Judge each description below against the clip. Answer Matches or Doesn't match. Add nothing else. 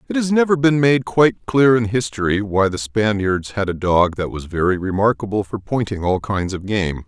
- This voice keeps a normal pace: Doesn't match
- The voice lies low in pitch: Matches